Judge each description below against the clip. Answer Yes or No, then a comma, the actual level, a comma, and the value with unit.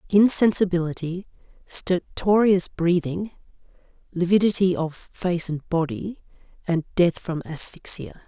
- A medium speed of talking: No, slow, 85 wpm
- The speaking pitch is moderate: Yes, medium, 180 Hz